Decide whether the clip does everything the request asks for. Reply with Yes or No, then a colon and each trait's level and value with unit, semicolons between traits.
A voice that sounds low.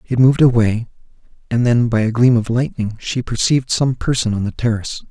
Yes: low, 120 Hz